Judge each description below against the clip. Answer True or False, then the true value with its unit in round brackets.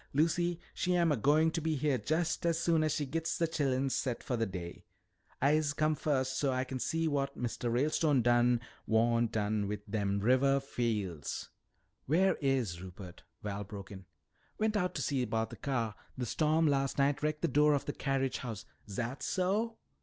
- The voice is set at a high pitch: False (135 Hz)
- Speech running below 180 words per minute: False (190 wpm)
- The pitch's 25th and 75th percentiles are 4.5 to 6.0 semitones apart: True (5.2 semitones)